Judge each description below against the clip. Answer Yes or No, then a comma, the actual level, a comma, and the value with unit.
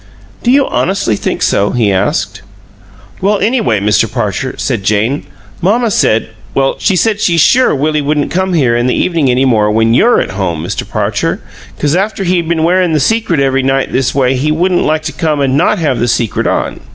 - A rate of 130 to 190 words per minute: No, average, 200 wpm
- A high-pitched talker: No, medium, 145 Hz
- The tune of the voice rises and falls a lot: Yes, wide, 6.8 semitones